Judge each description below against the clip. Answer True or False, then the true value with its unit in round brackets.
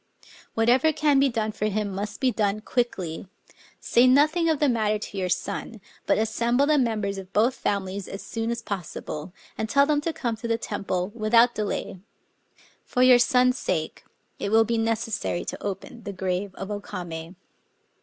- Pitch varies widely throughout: False (3.7 semitones)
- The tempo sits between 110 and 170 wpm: False (180 wpm)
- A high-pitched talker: True (220 Hz)